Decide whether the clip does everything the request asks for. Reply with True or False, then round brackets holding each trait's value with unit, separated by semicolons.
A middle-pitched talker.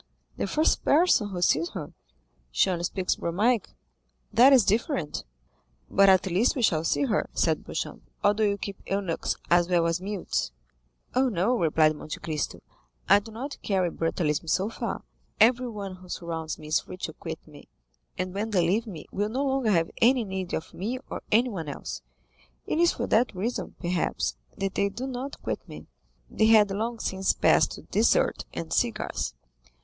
False (195 Hz)